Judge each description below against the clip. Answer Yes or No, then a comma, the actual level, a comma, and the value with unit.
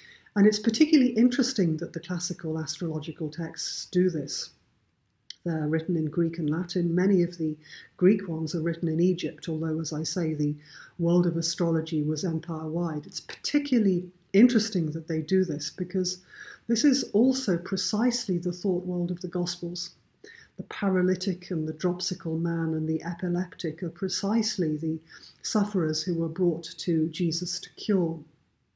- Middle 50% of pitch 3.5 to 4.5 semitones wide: No, narrow, 2.5 semitones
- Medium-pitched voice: Yes, medium, 175 Hz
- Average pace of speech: Yes, average, 155 wpm